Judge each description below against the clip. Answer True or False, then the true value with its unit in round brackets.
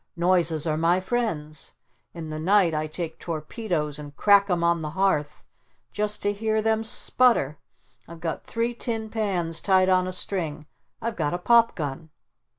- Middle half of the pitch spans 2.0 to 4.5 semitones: False (5.1 semitones)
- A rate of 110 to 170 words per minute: True (165 wpm)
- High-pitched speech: False (175 Hz)